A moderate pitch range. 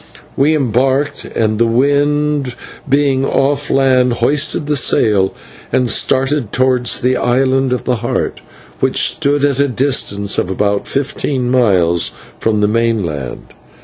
Yes: average, 3.5 semitones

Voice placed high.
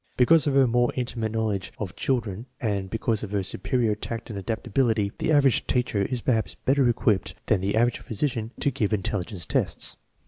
No: low, 115 Hz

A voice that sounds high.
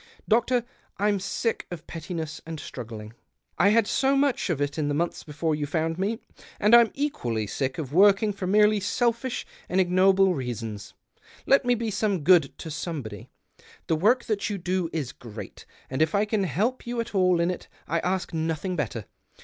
No: medium, 180 Hz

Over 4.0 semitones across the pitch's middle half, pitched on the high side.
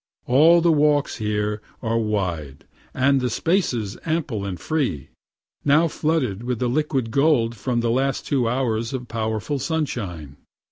No: average, 5.1 semitones; low, 125 Hz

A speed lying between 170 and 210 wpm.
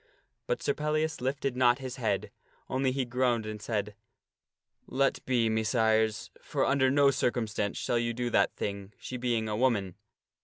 Yes: average, 175 wpm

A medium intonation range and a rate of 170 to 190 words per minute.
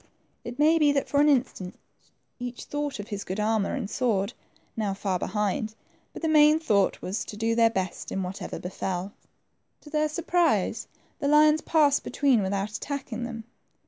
No: wide, 6.6 semitones; average, 175 wpm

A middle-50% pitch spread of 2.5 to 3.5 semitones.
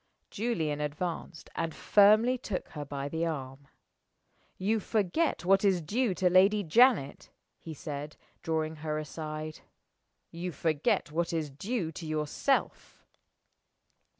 No: average, 4.5 semitones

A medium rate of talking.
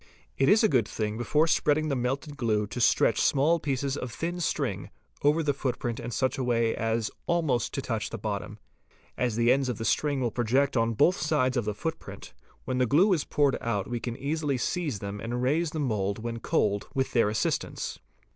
No: fast, 210 wpm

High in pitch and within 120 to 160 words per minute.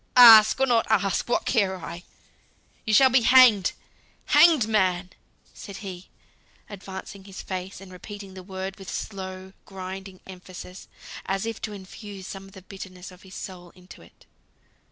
Yes: high, 195 Hz; average, 155 wpm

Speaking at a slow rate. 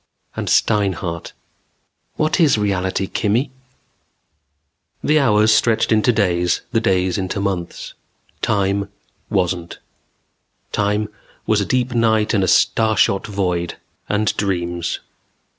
Yes: slow, 110 wpm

